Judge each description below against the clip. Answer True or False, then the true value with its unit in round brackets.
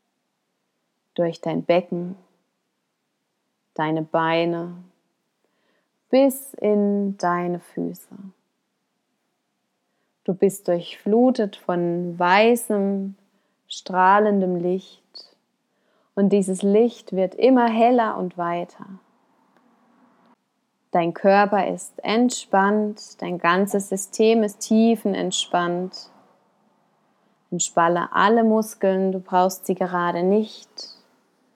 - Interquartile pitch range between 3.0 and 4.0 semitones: True (3.7 semitones)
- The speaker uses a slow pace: True (80 wpm)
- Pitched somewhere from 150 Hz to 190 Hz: False (200 Hz)